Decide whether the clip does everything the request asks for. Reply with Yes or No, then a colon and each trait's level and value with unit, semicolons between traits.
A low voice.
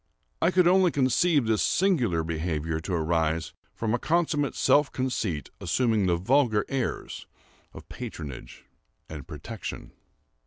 Yes: low, 115 Hz